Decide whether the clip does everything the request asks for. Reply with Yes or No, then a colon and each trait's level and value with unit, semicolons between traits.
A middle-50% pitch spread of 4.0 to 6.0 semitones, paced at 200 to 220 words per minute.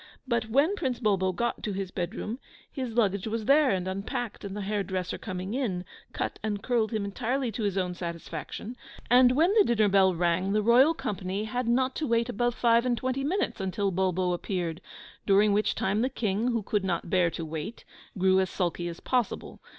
Yes: average, 4.4 semitones; fast, 205 wpm